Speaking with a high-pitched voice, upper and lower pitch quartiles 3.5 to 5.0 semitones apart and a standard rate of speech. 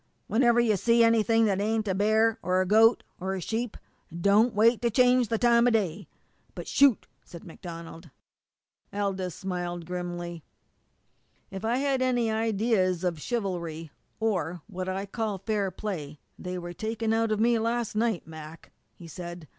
Yes: high, 205 Hz; average, 4.2 semitones; average, 160 wpm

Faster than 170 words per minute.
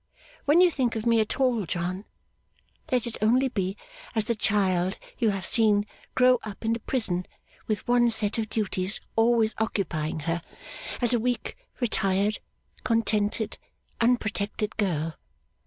No: average, 145 wpm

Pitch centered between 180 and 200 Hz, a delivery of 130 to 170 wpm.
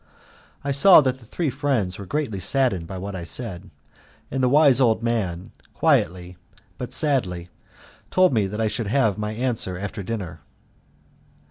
No: low, 110 Hz; average, 160 wpm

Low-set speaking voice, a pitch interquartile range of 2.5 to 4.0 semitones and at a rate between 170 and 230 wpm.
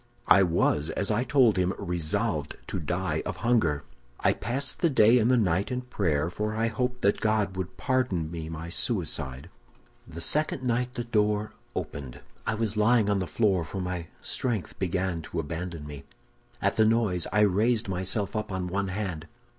No: low, 100 Hz; average, 4.9 semitones; average, 180 wpm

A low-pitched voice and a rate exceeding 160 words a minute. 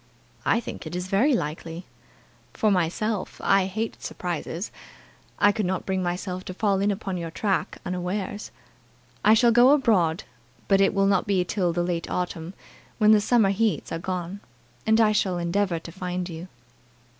No: high, 190 Hz; average, 170 wpm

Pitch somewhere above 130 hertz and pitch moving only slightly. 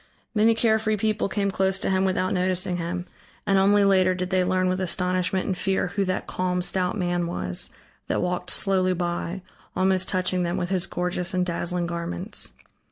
Yes: medium, 185 Hz; narrow, 1.2 semitones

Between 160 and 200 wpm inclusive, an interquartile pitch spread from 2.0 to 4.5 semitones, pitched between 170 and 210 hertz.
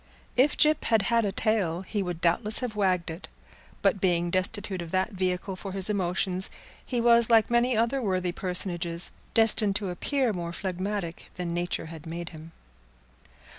Yes: average, 170 wpm; average, 3.9 semitones; high, 190 Hz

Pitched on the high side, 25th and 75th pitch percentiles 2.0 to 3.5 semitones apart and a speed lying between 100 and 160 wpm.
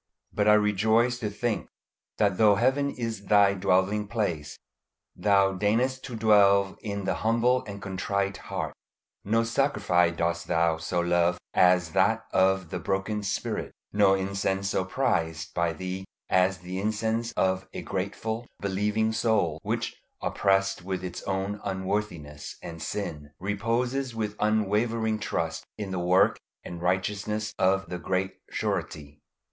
No: low, 100 Hz; average, 2.7 semitones; average, 140 wpm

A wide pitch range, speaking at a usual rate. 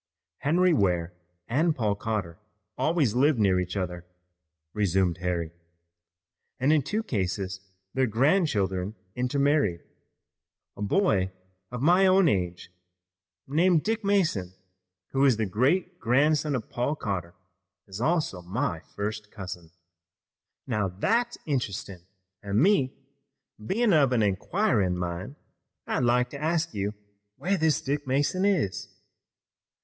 No: wide, 8.4 semitones; slow, 125 wpm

